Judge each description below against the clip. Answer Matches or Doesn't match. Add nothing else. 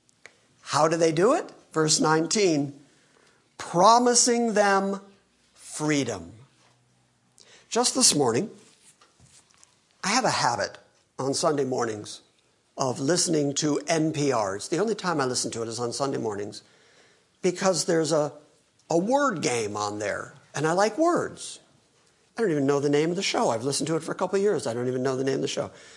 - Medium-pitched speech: Matches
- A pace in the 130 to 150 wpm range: Doesn't match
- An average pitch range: Doesn't match